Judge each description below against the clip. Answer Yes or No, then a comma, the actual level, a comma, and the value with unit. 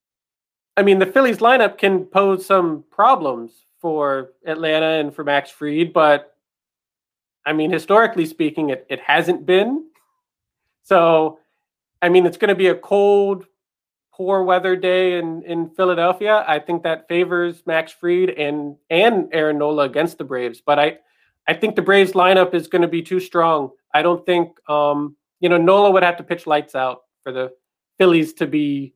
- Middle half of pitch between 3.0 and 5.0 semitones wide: Yes, average, 3.7 semitones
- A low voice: No, medium, 170 Hz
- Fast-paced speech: No, average, 170 wpm